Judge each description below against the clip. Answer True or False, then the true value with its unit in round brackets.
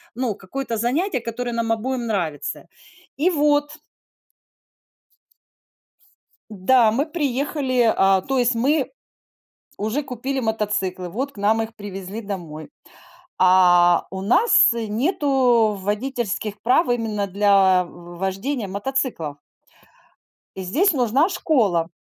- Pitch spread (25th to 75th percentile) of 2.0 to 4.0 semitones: False (5.4 semitones)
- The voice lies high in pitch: True (225 Hz)